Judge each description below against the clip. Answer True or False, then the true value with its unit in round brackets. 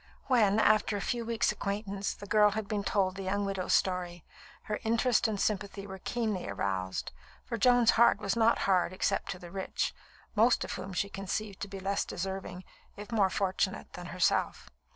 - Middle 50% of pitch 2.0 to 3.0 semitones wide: True (2.4 semitones)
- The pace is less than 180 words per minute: False (185 wpm)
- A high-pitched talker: True (200 Hz)